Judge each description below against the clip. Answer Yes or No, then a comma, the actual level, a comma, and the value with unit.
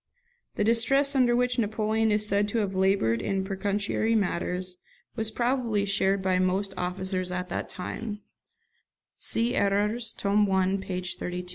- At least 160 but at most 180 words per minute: No, average, 145 wpm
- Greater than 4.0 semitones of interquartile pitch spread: No, average, 2.9 semitones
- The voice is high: Yes, high, 200 Hz